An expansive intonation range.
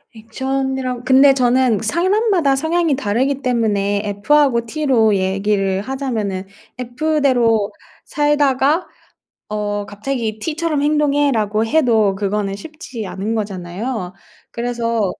No: average, 5.0 semitones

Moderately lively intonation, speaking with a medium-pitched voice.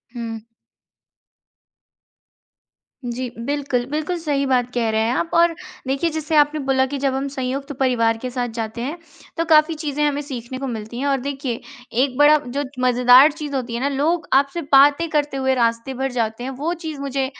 No: average, 3.0 semitones; very high, 270 Hz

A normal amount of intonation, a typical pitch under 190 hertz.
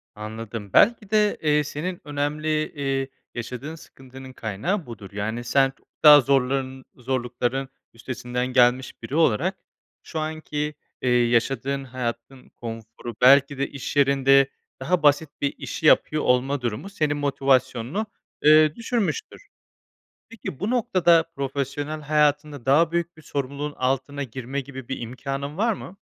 Yes: average, 3.3 semitones; medium, 140 Hz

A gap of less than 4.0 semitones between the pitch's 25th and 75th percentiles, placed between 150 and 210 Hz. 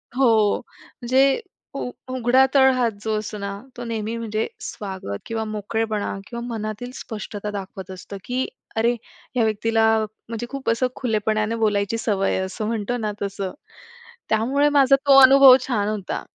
No: average, 2.8 semitones; high, 225 Hz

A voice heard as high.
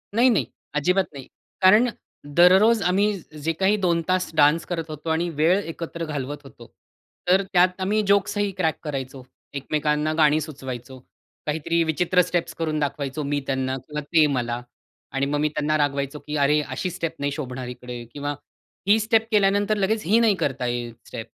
No: medium, 155 Hz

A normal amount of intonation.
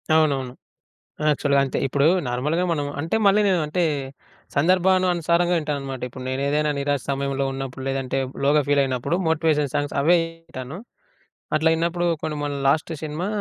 Yes: average, 3.3 semitones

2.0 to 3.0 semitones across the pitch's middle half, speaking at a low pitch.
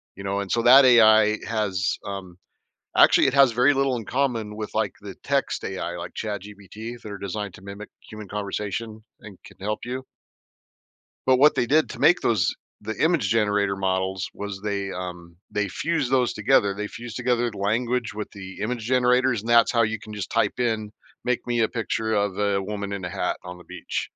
No: average, 3.4 semitones; low, 105 Hz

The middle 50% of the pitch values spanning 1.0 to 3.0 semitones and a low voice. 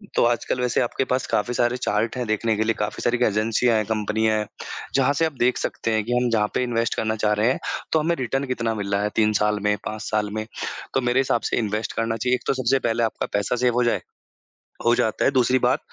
Yes: narrow, 2.5 semitones; low, 115 Hz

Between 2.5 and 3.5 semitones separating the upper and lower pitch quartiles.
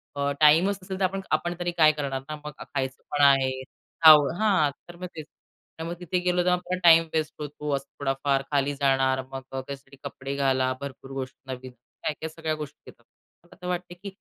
No: average, 4.2 semitones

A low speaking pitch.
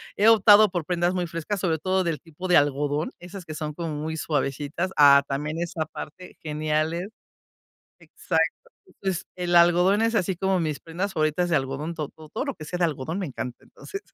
No: medium, 170 Hz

